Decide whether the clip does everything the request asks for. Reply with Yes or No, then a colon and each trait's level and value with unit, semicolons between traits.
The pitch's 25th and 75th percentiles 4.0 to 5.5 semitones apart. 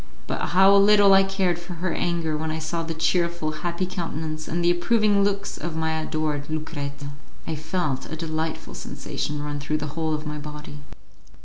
No: narrow, 2.4 semitones